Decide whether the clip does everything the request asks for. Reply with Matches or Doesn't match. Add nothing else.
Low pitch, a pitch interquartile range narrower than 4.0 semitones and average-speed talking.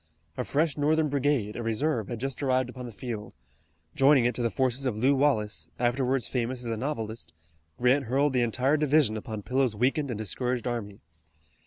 Matches